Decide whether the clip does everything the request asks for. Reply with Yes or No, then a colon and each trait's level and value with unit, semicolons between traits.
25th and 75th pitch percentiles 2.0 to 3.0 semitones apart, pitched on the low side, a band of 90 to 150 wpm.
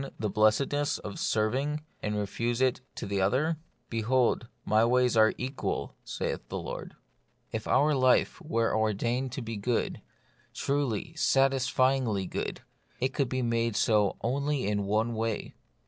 No: average, 3.6 semitones; low, 120 Hz; average, 145 wpm